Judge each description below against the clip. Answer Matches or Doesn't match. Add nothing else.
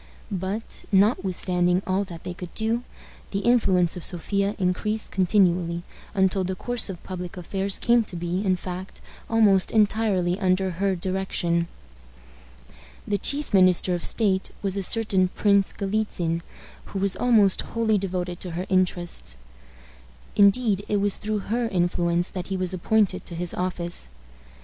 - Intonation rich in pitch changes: Doesn't match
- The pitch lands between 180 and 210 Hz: Matches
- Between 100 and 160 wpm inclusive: Matches